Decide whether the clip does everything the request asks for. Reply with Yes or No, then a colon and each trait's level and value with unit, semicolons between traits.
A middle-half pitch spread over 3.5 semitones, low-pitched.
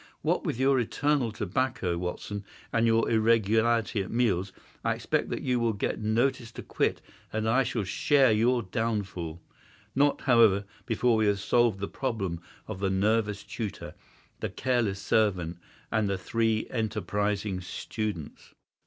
No: average, 2.9 semitones; low, 110 Hz